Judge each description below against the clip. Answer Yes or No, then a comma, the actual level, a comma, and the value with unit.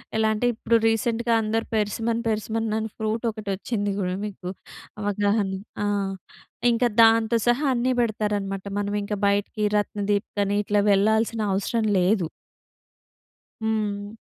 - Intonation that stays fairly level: Yes, narrow, 1.8 semitones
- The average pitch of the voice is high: Yes, high, 215 Hz